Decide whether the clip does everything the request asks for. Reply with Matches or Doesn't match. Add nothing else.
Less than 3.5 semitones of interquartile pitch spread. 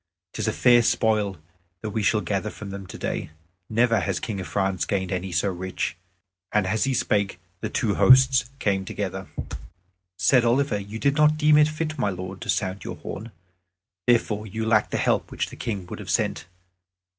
Doesn't match